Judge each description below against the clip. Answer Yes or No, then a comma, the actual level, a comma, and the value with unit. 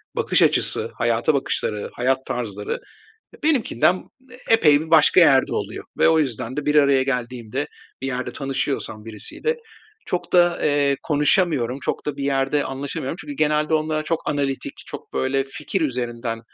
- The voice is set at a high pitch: No, medium, 140 Hz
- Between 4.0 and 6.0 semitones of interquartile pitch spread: No, average, 3.4 semitones